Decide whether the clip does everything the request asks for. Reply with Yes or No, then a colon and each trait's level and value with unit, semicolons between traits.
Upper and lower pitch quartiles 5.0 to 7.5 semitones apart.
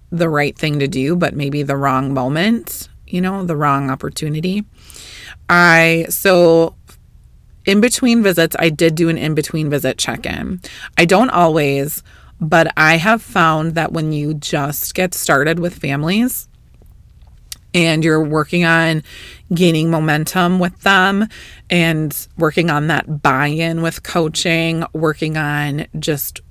No: narrow, 2.4 semitones